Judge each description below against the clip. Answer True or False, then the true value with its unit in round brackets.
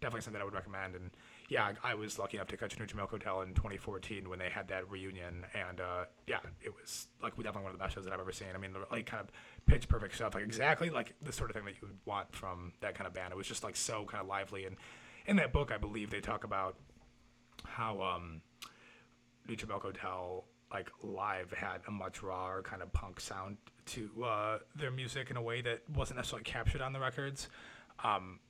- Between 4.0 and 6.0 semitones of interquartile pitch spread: False (3.3 semitones)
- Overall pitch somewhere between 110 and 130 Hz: False (100 Hz)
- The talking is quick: True (235 wpm)